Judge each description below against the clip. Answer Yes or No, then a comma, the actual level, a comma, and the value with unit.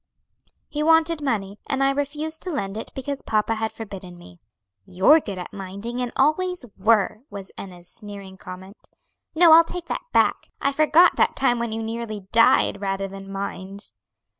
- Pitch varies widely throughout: Yes, wide, 6.6 semitones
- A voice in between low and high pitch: No, high, 225 Hz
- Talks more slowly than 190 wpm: Yes, average, 170 wpm